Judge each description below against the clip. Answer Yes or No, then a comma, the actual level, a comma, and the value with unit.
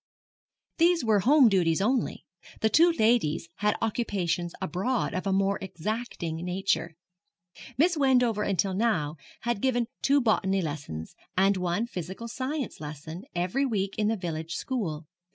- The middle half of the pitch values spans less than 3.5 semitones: No, wide, 5.5 semitones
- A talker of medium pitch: No, high, 200 Hz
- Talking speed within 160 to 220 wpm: No, average, 140 wpm